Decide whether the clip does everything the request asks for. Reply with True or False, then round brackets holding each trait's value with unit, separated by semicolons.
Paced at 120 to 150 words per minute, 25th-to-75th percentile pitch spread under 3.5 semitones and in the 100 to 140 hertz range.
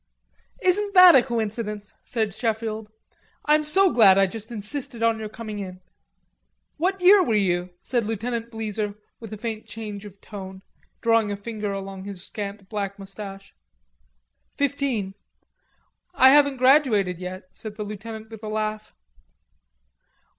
False (140 wpm; 3.1 semitones; 215 Hz)